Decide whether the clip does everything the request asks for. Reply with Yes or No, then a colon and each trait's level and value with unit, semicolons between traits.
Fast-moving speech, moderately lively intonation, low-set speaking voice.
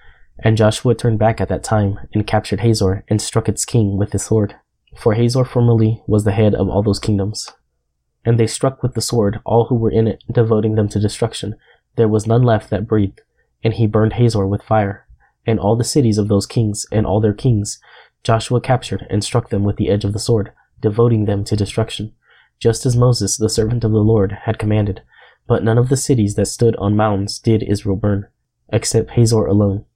No: fast, 210 wpm; narrow, 2.1 semitones; low, 110 Hz